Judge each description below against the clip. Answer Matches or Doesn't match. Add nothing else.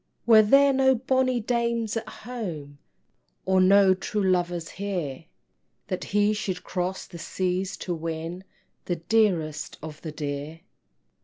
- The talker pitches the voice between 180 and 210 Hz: Matches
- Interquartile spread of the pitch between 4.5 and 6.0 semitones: Matches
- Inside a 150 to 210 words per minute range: Doesn't match